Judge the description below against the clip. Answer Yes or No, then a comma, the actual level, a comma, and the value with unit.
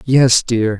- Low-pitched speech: Yes, low, 120 Hz